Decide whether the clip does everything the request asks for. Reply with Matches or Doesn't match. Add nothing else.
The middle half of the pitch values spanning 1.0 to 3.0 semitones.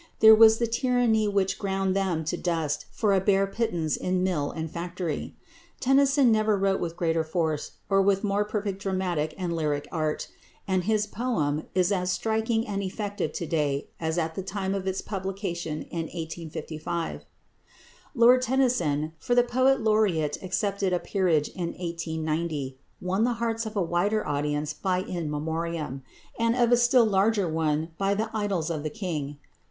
Doesn't match